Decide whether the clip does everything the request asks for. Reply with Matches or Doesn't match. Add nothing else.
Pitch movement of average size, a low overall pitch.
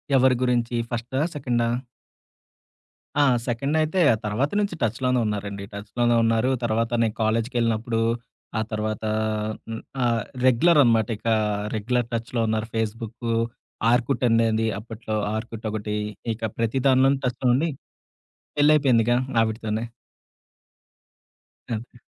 Doesn't match